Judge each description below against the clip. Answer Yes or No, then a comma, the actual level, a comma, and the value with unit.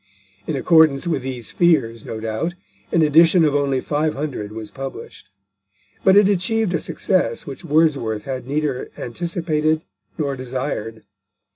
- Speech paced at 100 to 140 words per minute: Yes, slow, 135 wpm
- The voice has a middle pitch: Yes, medium, 145 Hz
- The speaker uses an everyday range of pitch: Yes, average, 4.4 semitones